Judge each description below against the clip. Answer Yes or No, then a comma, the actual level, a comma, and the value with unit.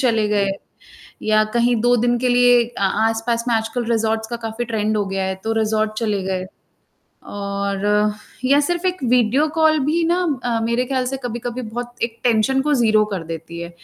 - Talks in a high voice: Yes, high, 230 Hz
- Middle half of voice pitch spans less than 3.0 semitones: Yes, narrow, 2.5 semitones